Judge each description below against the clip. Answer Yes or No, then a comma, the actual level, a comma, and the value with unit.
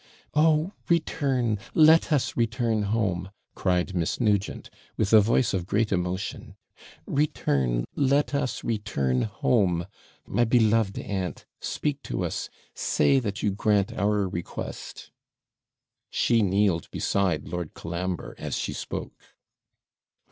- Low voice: Yes, low, 105 Hz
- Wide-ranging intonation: No, average, 4.7 semitones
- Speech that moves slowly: Yes, slow, 120 wpm